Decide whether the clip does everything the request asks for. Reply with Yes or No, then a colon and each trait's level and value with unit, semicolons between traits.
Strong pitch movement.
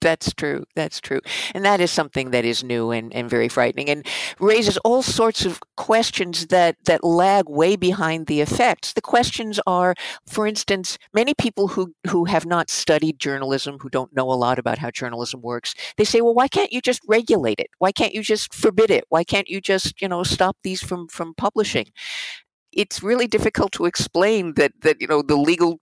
Yes: wide, 5.9 semitones